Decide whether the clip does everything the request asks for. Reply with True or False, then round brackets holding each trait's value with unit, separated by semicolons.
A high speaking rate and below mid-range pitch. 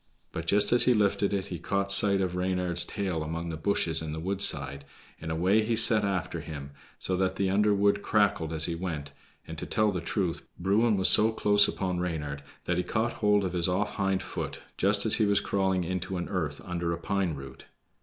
True (215 wpm; 95 Hz)